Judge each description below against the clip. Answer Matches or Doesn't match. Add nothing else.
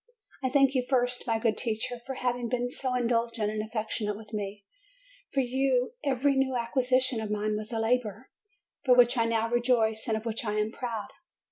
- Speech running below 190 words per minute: Doesn't match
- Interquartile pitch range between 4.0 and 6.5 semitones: Doesn't match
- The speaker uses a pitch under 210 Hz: Doesn't match